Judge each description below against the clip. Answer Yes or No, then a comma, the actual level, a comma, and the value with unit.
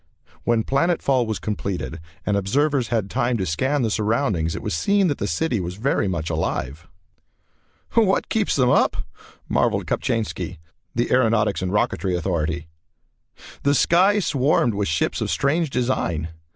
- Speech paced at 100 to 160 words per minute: Yes, average, 150 wpm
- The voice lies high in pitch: No, low, 115 Hz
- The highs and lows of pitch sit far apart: Yes, wide, 7.4 semitones